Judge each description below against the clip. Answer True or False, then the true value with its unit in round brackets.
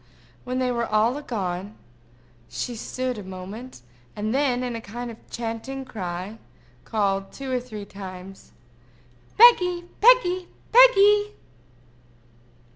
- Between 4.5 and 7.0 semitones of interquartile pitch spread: True (5.2 semitones)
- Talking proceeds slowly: True (120 wpm)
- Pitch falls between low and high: False (240 Hz)